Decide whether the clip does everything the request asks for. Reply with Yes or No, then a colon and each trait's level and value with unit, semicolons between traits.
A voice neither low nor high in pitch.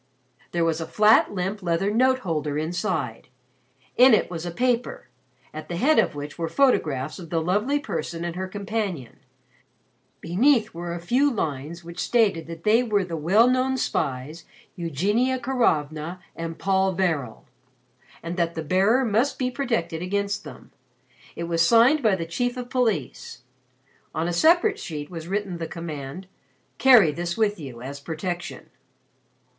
Yes: medium, 175 Hz